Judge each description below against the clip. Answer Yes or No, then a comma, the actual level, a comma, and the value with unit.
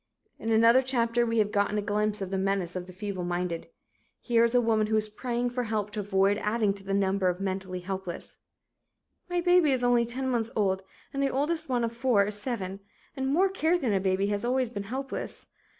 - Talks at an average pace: No, fast, 215 wpm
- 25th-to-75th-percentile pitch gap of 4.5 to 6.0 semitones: No, average, 3.9 semitones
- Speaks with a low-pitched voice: No, high, 215 Hz